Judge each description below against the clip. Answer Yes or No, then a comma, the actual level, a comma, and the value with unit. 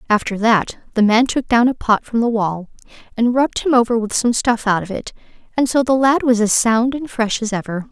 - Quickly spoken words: Yes, fast, 240 wpm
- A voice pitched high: Yes, high, 230 Hz